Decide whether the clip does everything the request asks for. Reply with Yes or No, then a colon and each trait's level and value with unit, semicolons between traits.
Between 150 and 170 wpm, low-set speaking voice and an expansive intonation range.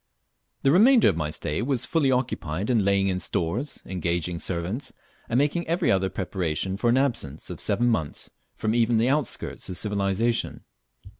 Yes: average, 165 wpm; low, 105 Hz; wide, 6.0 semitones